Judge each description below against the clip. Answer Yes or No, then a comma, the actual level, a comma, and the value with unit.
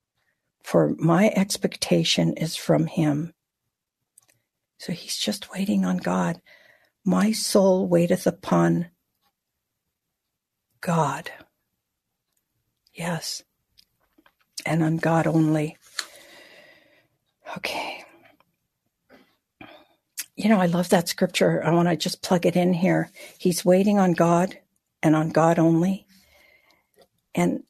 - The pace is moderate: No, slow, 100 wpm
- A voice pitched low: No, medium, 170 Hz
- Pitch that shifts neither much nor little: Yes, average, 3.1 semitones